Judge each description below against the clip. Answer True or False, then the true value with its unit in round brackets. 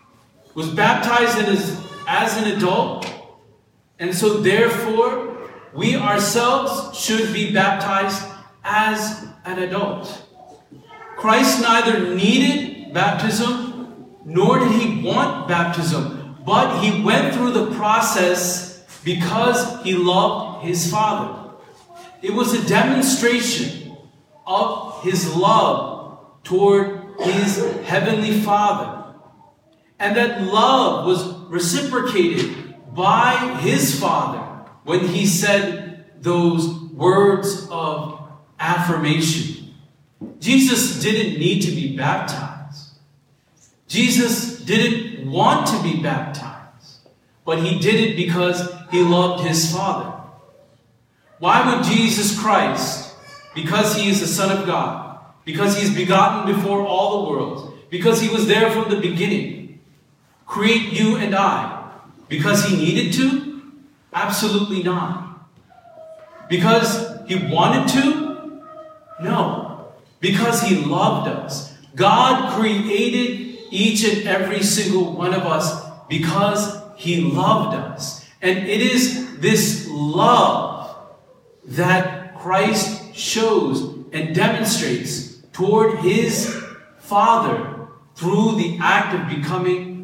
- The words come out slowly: True (105 wpm)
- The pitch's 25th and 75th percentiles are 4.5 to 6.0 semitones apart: False (4.0 semitones)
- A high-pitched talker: True (195 Hz)